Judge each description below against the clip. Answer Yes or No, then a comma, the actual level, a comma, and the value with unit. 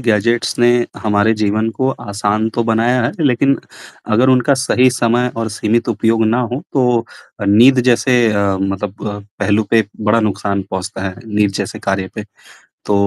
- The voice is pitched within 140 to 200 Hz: No, low, 110 Hz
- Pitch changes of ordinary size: Yes, average, 3.0 semitones